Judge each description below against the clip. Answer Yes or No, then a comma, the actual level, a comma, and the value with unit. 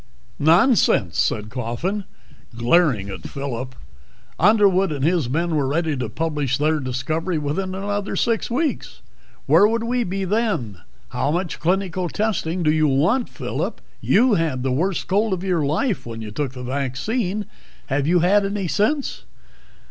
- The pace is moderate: Yes, average, 155 wpm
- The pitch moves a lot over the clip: Yes, wide, 6.5 semitones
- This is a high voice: No, medium, 170 Hz